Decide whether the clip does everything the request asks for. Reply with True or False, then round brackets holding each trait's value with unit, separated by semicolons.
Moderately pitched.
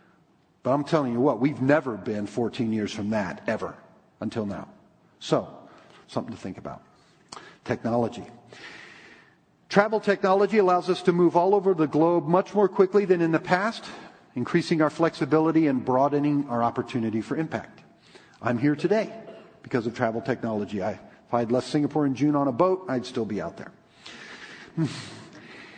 True (150 Hz)